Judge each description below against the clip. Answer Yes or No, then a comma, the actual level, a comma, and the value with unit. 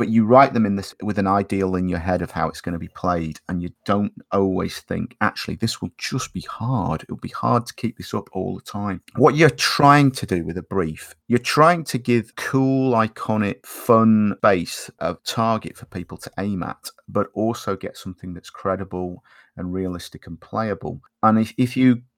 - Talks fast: Yes, fast, 210 wpm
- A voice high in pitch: No, low, 100 Hz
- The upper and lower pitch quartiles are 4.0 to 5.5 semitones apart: Yes, average, 4.8 semitones